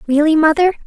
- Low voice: No, very high, 315 Hz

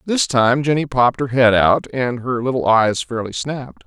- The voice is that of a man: Yes, male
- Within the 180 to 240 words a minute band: Yes, average, 200 wpm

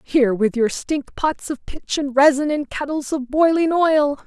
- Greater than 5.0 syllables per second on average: No, 4.4 syllables/s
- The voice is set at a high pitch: Yes, very high, 285 Hz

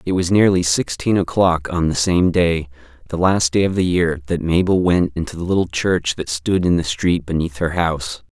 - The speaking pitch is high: No, very low, 85 Hz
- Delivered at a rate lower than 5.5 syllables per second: Yes, 5.0 syllables/s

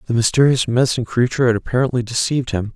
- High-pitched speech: No, low, 120 Hz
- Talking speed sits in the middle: Yes, average, 175 wpm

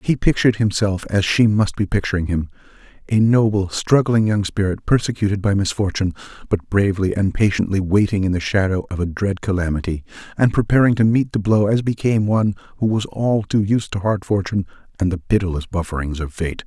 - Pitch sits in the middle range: No, low, 100 Hz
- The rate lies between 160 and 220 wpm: Yes, average, 185 wpm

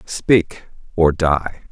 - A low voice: Yes, very low, 85 Hz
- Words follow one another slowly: Yes, slow, 105 wpm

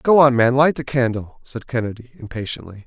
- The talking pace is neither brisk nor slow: Yes, average, 190 wpm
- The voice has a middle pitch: No, low, 125 Hz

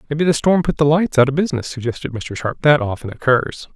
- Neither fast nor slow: No, fast, 240 wpm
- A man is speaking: Yes, male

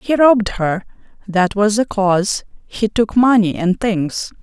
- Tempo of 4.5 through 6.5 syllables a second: No, 4.1 syllables/s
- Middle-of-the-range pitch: No, high, 210 Hz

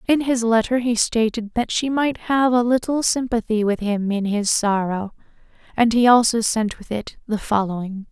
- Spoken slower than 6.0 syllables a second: Yes, 4.7 syllables/s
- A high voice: Yes, high, 225 Hz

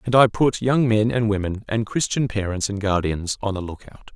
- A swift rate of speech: Yes, fast, 230 wpm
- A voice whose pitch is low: Yes, low, 110 Hz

